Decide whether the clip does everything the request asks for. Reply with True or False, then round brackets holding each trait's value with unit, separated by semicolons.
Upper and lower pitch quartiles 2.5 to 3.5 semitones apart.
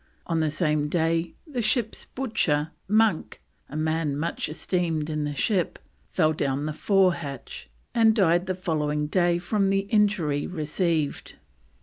False (4.3 semitones)